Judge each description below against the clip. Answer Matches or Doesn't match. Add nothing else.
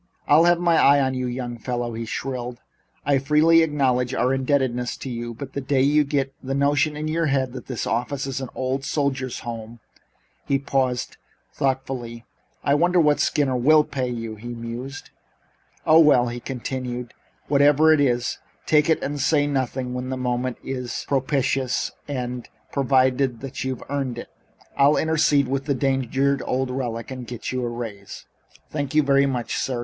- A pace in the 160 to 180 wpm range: Matches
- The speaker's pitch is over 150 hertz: Doesn't match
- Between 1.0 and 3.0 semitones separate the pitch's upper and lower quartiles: Matches